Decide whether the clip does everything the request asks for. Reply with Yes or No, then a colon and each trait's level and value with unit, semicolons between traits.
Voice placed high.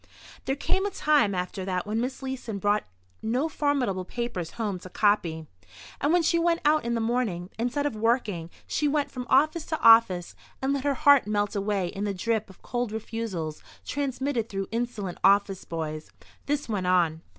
Yes: high, 225 Hz